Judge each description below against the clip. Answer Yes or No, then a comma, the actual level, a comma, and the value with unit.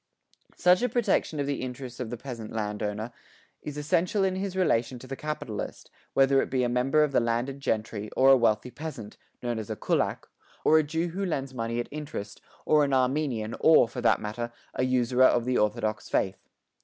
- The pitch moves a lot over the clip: No, average, 4.7 semitones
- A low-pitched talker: Yes, low, 130 Hz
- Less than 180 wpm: No, average, 200 wpm